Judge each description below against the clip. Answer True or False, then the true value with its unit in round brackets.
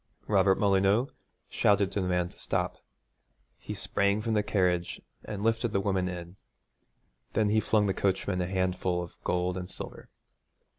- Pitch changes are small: True (2.3 semitones)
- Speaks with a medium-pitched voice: False (95 Hz)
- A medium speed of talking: True (160 wpm)